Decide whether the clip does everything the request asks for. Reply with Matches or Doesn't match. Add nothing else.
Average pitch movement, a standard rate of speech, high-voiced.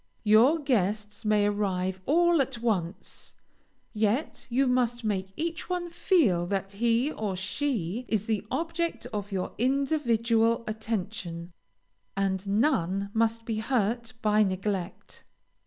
Doesn't match